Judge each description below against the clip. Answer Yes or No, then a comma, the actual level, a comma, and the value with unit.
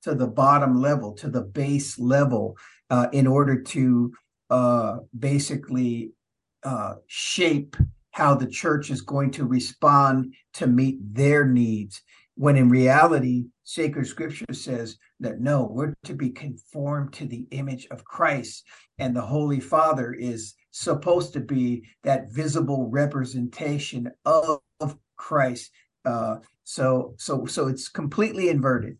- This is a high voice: No, low, 135 Hz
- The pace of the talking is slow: Yes, slow, 130 wpm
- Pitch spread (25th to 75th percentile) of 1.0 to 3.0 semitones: Yes, narrow, 2.6 semitones